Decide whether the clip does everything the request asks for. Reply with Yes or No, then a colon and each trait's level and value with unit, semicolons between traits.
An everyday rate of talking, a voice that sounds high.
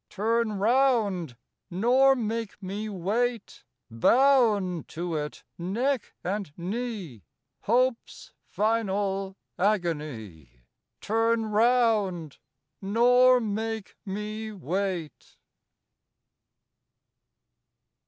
No: slow, 70 wpm; high, 210 Hz